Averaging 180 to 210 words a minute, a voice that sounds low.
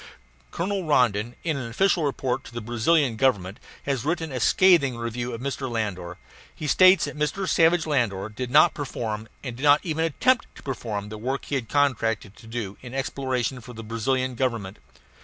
Yes: average, 185 wpm; low, 125 Hz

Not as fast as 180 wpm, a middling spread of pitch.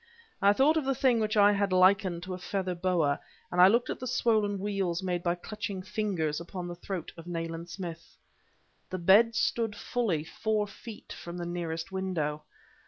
No: average, 185 wpm; average, 3.4 semitones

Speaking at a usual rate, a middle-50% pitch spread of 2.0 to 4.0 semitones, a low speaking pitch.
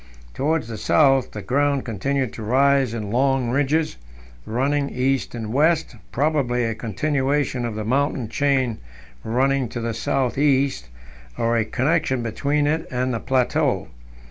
Yes: average, 145 wpm; average, 3.2 semitones; low, 130 Hz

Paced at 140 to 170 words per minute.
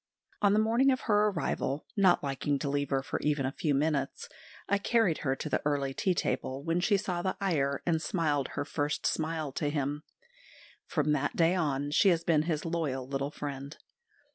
No: average, 195 wpm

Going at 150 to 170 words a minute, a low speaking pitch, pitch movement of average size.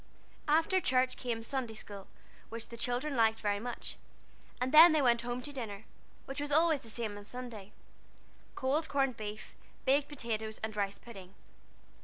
No: average, 165 wpm; high, 240 Hz; average, 3.9 semitones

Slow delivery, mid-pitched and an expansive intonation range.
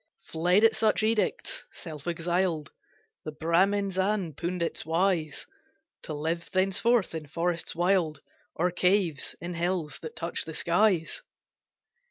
No: slow, 130 wpm; medium, 175 Hz; average, 2.9 semitones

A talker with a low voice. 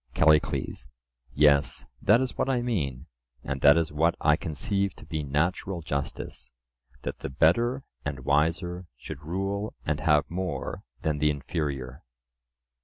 Yes: very low, 75 Hz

